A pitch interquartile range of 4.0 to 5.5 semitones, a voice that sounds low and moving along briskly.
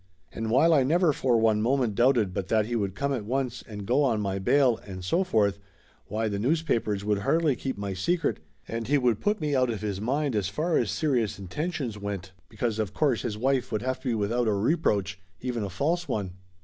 Yes: average, 5.1 semitones; low, 115 Hz; fast, 225 wpm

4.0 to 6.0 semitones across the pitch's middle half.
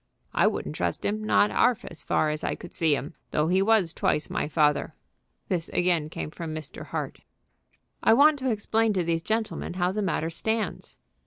Yes: wide, 5.5 semitones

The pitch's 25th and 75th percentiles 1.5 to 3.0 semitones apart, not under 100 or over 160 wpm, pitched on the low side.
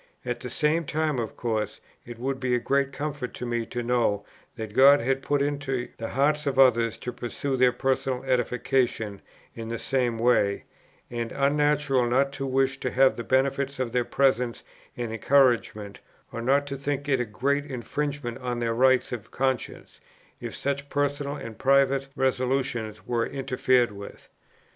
No: narrow, 2.5 semitones; average, 170 wpm; low, 130 Hz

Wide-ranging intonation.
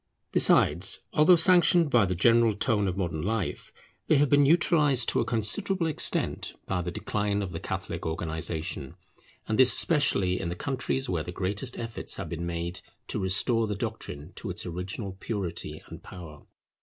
Yes: wide, 6.8 semitones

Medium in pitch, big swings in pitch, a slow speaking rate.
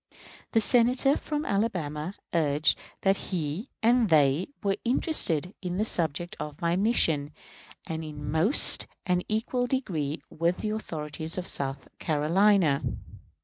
Yes: medium, 175 Hz; wide, 6.0 semitones; slow, 125 wpm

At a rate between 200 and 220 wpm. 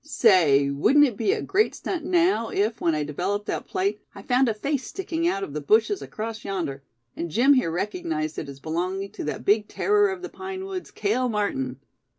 Yes: fast, 205 wpm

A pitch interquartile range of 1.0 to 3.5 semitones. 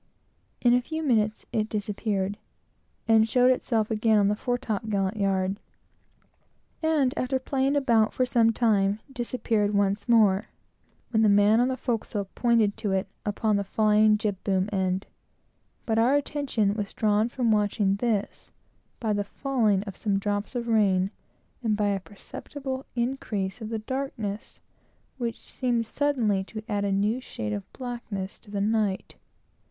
Yes: average, 3.1 semitones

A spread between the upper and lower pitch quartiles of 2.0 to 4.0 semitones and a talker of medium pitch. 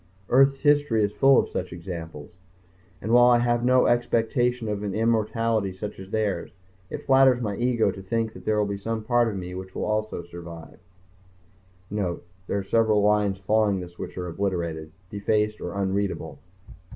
No: average, 3.4 semitones; low, 105 Hz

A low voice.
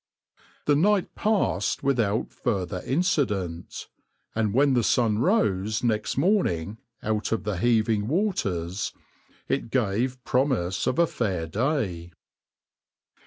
Yes: low, 110 Hz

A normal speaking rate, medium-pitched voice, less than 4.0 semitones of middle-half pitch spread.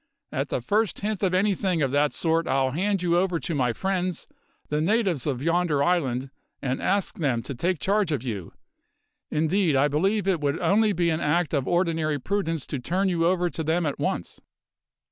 No: average, 195 wpm; medium, 165 Hz; average, 4.6 semitones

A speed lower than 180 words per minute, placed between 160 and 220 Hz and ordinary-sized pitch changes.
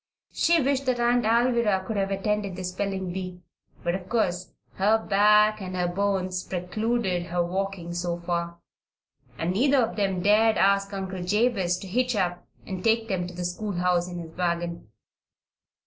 Yes: average, 165 wpm; high, 190 Hz; average, 3.2 semitones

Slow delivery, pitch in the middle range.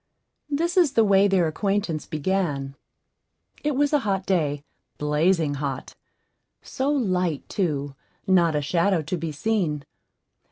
Yes: slow, 130 wpm; medium, 180 Hz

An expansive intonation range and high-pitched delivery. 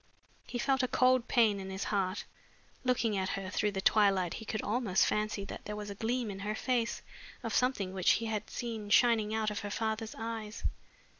No: narrow, 2.4 semitones; high, 215 Hz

